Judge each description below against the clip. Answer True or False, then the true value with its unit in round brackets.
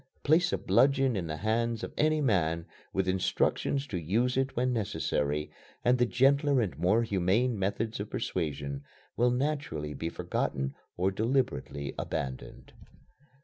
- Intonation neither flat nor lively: False (7.3 semitones)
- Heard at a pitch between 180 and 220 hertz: False (110 Hz)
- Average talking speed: True (145 wpm)